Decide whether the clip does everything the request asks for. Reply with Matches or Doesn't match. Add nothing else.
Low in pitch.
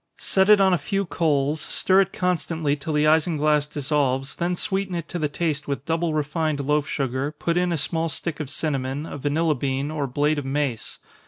Doesn't match